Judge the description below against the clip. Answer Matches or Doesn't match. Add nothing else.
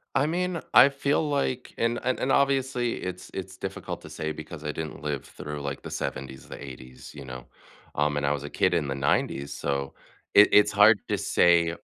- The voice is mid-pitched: Doesn't match